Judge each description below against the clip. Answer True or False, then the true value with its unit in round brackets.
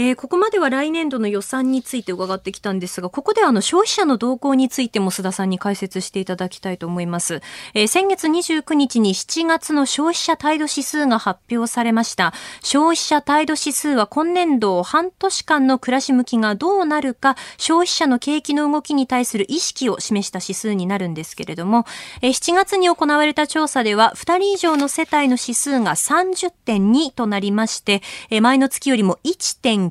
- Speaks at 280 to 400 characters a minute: True (350 characters per minute)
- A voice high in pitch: True (260 Hz)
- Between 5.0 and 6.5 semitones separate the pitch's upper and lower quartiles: False (7.1 semitones)